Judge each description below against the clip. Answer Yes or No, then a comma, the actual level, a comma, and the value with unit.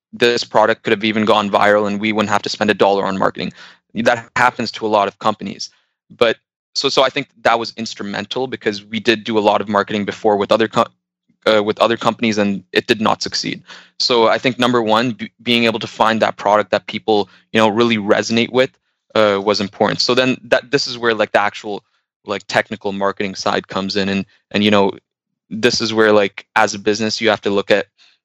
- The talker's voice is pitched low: Yes, low, 110 Hz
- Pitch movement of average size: No, narrow, 2.1 semitones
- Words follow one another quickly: Yes, fast, 225 wpm